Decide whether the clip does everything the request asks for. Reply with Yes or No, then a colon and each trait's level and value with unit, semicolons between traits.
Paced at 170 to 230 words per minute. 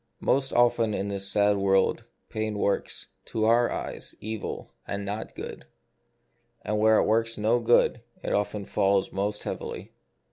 No: average, 150 wpm